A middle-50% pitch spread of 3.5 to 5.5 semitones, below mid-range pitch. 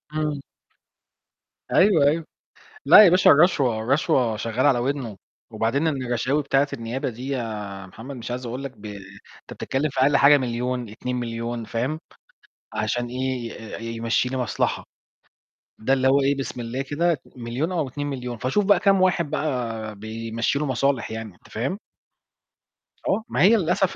Yes: average, 3.8 semitones; low, 130 Hz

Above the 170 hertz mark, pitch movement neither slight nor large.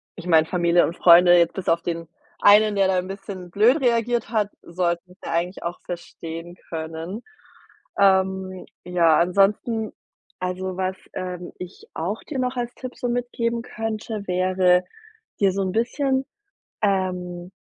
Yes: medium, 185 Hz; average, 3.5 semitones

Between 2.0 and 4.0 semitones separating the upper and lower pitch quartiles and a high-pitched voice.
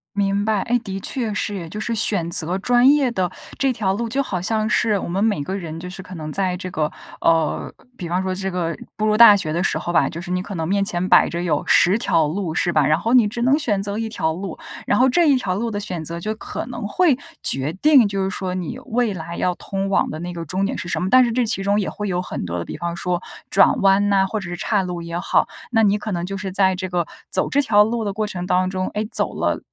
Yes: average, 3.6 semitones; high, 195 Hz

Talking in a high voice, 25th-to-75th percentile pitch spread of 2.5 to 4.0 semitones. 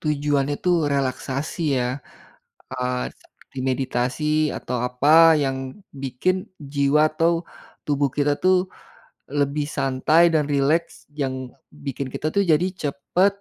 No: medium, 145 Hz; average, 2.8 semitones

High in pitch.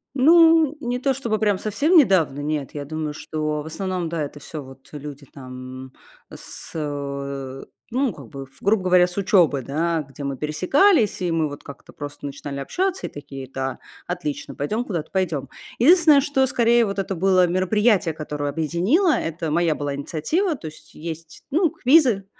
No: medium, 165 Hz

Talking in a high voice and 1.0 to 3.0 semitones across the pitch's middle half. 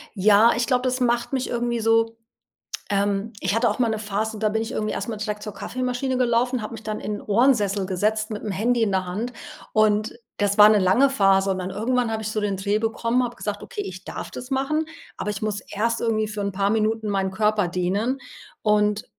Yes: high, 215 Hz; narrow, 2.6 semitones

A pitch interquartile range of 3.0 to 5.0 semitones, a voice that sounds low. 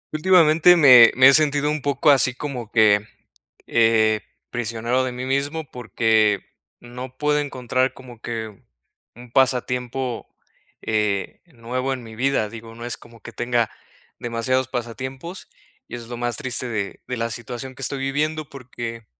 No: narrow, 2.6 semitones; low, 125 Hz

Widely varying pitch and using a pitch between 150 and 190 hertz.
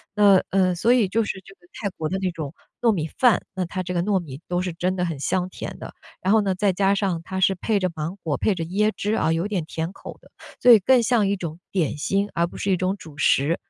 No: average, 3.0 semitones; medium, 185 Hz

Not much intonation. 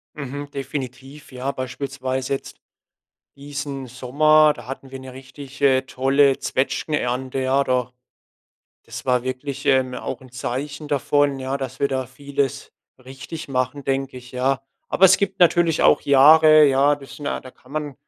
Yes: narrow, 1.7 semitones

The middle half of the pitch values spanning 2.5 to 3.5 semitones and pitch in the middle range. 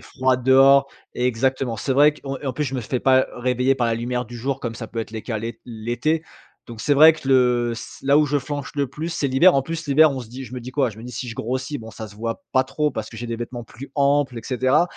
No: average, 2.8 semitones; low, 130 Hz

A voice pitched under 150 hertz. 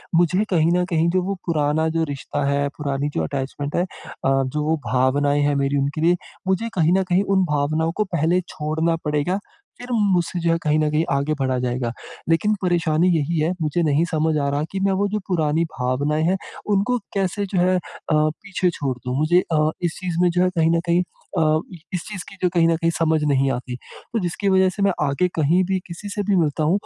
No: medium, 160 Hz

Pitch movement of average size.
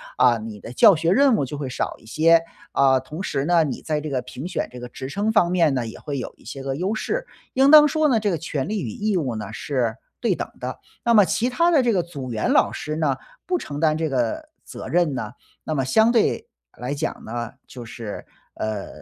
No: wide, 8.1 semitones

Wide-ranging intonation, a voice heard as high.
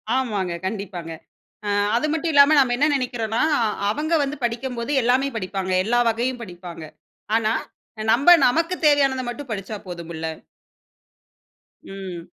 Yes: wide, 5.9 semitones; high, 235 Hz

